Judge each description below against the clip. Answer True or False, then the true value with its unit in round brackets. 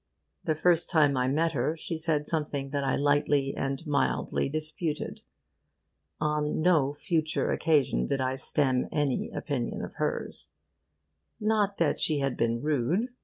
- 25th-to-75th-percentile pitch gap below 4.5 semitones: True (2.6 semitones)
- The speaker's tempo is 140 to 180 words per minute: True (145 wpm)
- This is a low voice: False (150 Hz)